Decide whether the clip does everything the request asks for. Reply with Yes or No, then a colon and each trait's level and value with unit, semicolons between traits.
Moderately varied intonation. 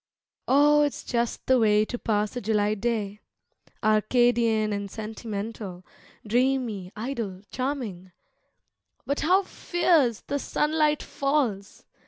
Yes: average, 4.5 semitones